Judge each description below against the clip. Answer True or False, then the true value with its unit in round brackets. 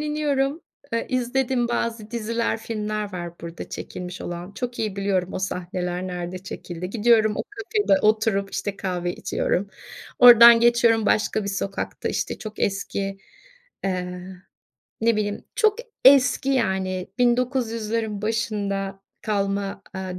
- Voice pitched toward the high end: True (210 Hz)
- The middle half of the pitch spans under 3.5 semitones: False (3.8 semitones)